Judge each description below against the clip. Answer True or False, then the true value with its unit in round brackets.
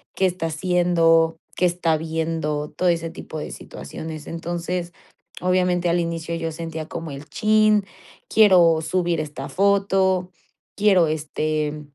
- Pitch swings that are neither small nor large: False (2.2 semitones)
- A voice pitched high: False (165 Hz)